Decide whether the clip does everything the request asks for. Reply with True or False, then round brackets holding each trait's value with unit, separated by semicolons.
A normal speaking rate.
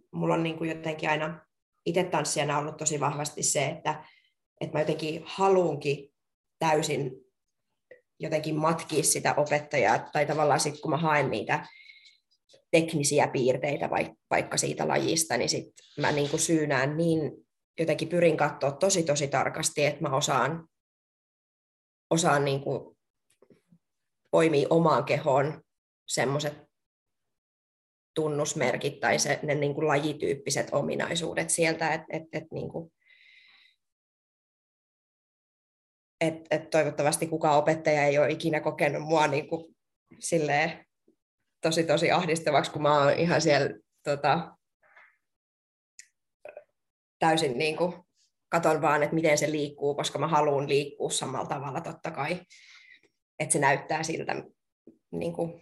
True (120 wpm)